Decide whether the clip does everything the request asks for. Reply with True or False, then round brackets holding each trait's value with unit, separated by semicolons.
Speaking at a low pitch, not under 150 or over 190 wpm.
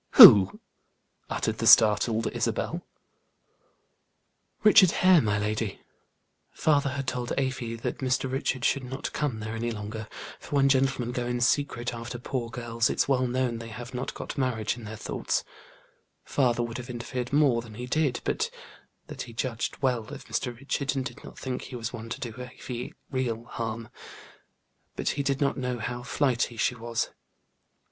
True (125 Hz; 170 wpm)